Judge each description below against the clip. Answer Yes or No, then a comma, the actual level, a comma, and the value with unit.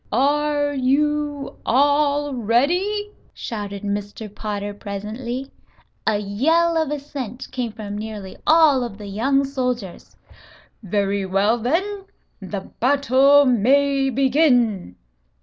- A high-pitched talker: Yes, very high, 255 Hz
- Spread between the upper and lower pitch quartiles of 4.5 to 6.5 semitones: Yes, wide, 5.5 semitones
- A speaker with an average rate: No, slow, 105 wpm